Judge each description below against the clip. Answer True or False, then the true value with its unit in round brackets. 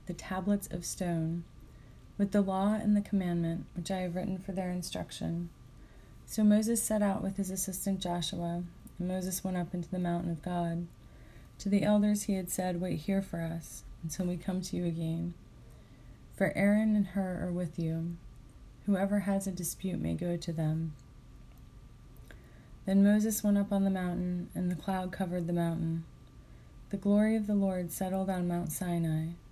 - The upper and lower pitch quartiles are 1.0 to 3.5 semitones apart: True (2.8 semitones)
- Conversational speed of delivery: True (175 wpm)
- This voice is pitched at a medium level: True (180 Hz)